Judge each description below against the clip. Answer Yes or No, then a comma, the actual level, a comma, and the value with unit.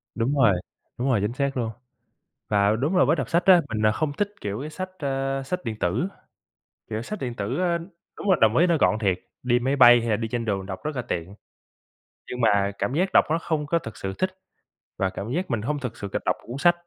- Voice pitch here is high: No, low, 125 Hz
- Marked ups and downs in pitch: Yes, wide, 6.3 semitones